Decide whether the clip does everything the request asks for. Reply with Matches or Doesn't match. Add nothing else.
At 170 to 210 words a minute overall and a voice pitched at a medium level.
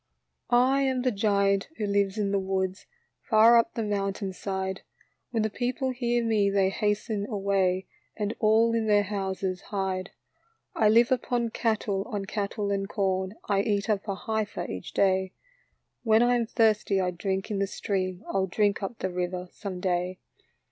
Doesn't match